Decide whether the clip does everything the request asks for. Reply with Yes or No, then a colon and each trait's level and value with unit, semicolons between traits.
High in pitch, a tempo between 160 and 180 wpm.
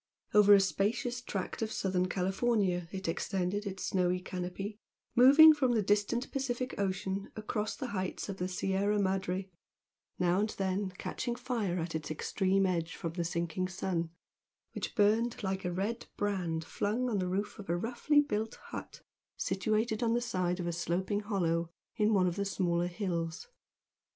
Yes: high, 195 Hz; average, 165 wpm